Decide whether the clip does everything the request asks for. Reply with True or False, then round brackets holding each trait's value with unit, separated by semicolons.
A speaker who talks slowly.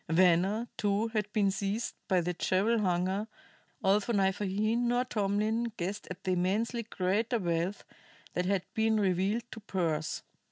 False (150 wpm)